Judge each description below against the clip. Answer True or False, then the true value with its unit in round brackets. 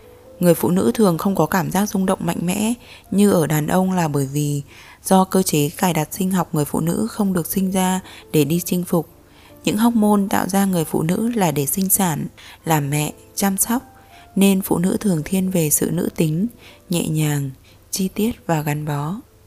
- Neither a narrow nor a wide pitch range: True (4.3 semitones)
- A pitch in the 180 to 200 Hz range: True (185 Hz)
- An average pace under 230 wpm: True (215 wpm)